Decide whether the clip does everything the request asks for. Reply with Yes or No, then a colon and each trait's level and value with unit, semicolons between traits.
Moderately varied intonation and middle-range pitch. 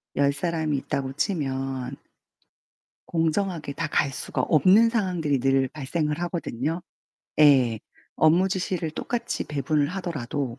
Yes: average, 4.3 semitones; medium, 150 Hz